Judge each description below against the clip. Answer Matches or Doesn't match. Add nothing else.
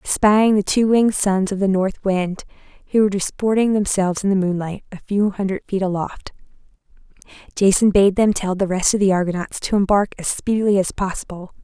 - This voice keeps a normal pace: Matches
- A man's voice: Doesn't match